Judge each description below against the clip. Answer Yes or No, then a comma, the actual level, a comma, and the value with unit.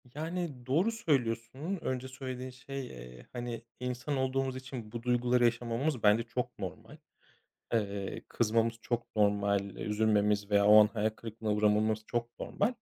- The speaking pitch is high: No, low, 120 Hz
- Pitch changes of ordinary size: Yes, average, 3.4 semitones